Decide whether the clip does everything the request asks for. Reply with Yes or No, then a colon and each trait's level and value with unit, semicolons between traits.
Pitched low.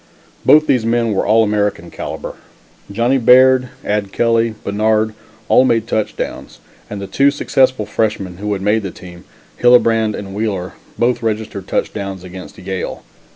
Yes: low, 110 Hz